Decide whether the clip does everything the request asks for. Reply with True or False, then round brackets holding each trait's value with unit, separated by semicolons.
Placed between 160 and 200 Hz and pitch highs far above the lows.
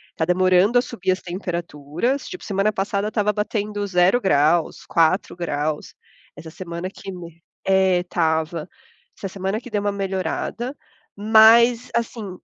False (190 Hz; 3.6 semitones)